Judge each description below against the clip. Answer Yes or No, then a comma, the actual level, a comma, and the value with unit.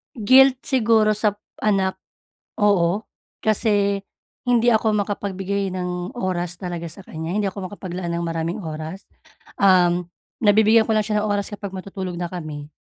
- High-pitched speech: Yes, high, 195 Hz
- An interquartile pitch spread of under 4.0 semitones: Yes, average, 3.2 semitones